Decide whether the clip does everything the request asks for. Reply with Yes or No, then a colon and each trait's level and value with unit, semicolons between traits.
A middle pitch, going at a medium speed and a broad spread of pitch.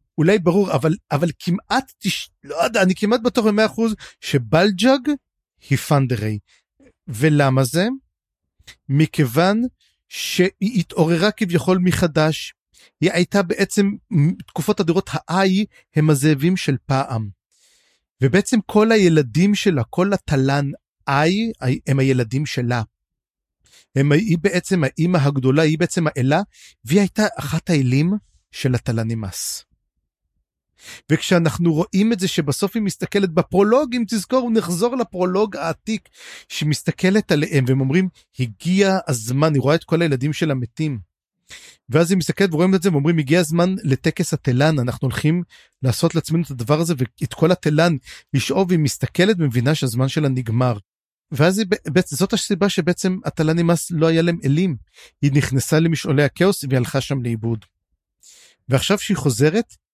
Yes: medium, 165 Hz; average, 135 wpm; wide, 5.7 semitones